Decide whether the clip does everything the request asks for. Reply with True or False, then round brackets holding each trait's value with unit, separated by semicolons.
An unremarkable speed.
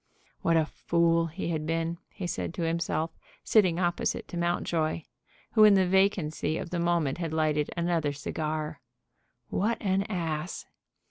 True (150 wpm)